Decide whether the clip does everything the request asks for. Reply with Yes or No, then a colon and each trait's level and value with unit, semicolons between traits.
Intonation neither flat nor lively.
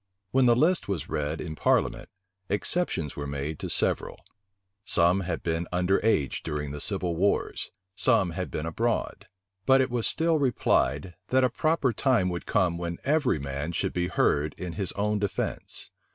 No: wide, 6.8 semitones